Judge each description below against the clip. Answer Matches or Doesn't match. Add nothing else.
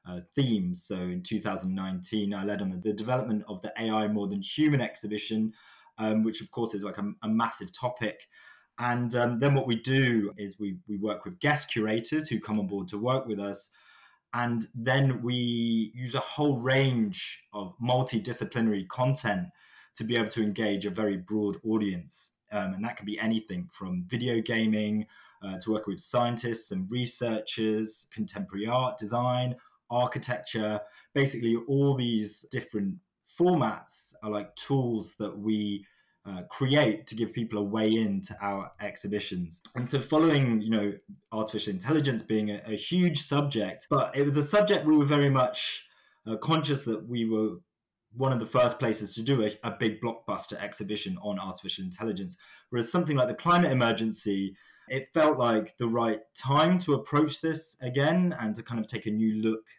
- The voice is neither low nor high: Doesn't match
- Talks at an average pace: Matches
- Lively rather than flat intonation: Doesn't match